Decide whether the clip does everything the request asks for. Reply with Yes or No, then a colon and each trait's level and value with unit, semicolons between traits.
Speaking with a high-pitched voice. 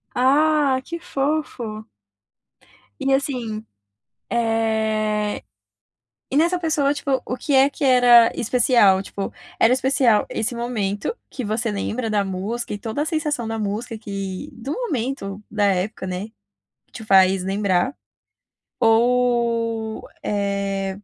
Yes: high, 230 Hz